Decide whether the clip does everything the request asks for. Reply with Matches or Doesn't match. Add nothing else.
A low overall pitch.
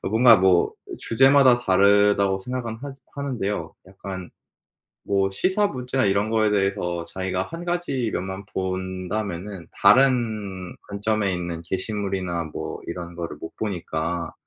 Matches